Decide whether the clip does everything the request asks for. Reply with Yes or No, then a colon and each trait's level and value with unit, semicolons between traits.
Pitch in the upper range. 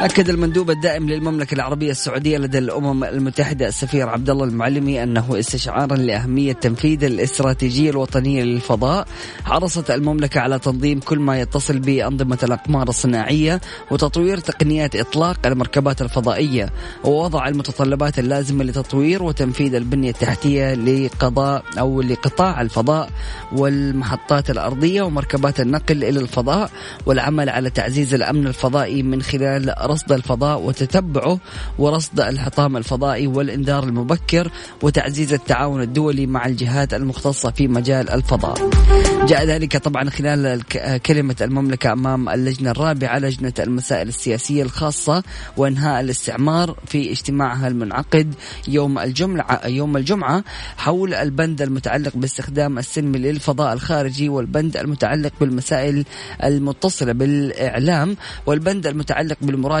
No: medium, 140 Hz